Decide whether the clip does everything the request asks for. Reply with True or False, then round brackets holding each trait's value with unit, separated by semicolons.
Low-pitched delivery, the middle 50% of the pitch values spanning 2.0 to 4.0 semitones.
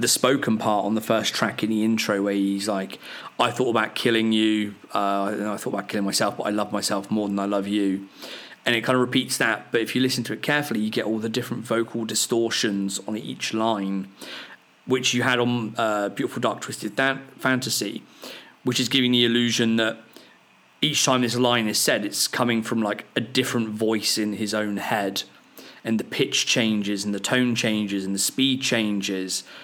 True (110 Hz; 2.9 semitones)